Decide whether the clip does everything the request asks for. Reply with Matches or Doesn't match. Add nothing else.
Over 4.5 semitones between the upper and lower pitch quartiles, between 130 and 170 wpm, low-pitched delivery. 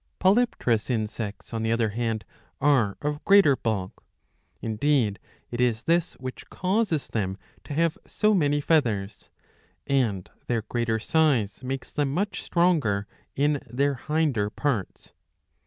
Matches